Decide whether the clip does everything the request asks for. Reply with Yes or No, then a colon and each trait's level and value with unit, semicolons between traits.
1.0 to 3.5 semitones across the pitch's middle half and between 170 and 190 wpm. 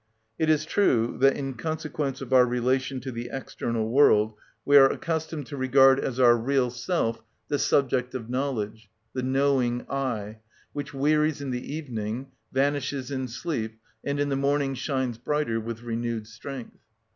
No: average, 3.1 semitones; average, 160 wpm